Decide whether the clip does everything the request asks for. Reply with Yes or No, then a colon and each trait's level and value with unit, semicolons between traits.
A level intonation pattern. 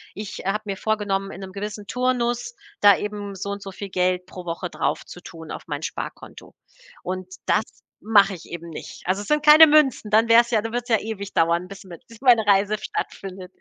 No: average, 3.2 semitones